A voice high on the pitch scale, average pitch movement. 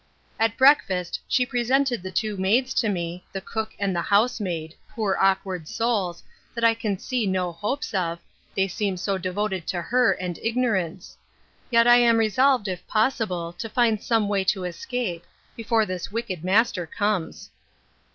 Yes: high, 205 Hz; average, 4.1 semitones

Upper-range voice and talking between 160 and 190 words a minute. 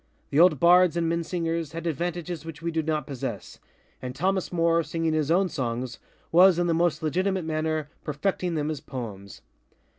No: medium, 165 Hz; average, 170 wpm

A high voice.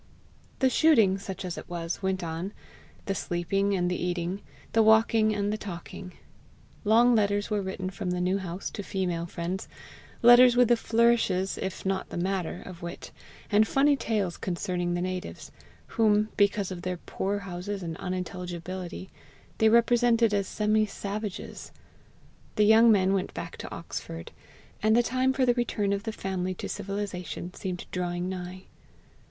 Yes: high, 195 Hz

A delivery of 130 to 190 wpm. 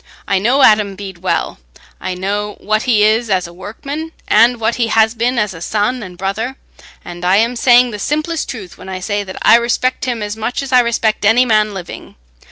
No: fast, 205 wpm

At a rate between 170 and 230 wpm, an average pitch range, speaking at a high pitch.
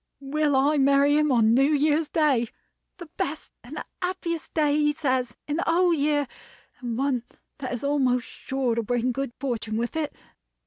Yes: average, 175 wpm; average, 3.3 semitones; very high, 280 Hz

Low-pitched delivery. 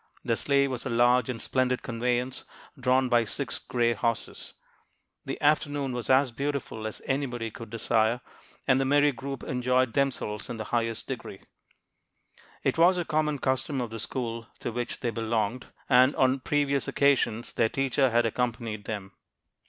Yes: low, 125 Hz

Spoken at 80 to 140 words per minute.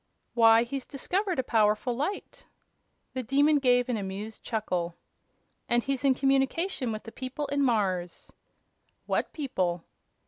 Yes: slow, 135 wpm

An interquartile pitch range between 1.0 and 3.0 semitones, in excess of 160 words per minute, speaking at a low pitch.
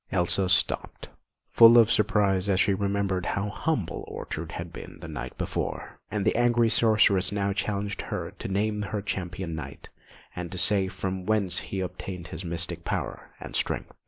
Yes: narrow, 2.5 semitones; average, 170 wpm; low, 100 Hz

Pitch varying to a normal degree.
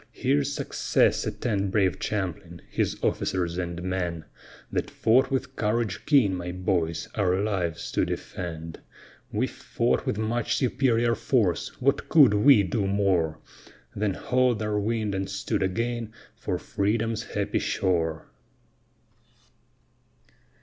Yes: average, 4.2 semitones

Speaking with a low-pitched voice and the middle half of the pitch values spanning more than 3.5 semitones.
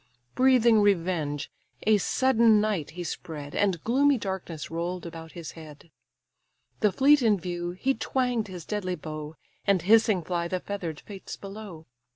No: medium, 185 Hz; average, 4.7 semitones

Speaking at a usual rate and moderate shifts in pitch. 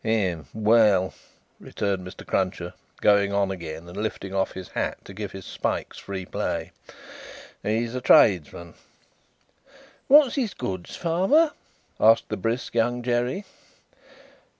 No: slow, 125 wpm; average, 4.3 semitones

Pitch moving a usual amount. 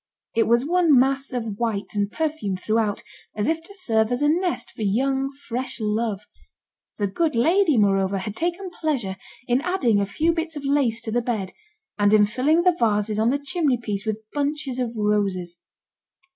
No: wide, 5.9 semitones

